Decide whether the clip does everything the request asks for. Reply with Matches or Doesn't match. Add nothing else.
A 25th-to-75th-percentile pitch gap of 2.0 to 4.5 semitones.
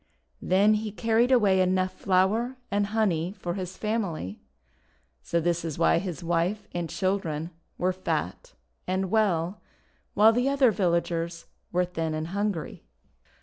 Matches